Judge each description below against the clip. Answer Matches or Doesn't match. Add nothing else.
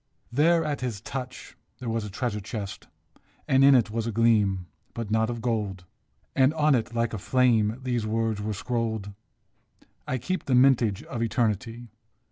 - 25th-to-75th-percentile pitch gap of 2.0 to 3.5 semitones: Matches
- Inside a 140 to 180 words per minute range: Matches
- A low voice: Matches